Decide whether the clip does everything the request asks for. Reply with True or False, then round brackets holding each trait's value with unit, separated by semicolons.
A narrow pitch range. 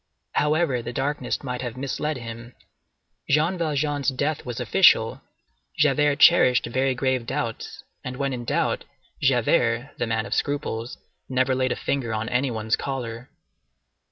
False (3.2 semitones)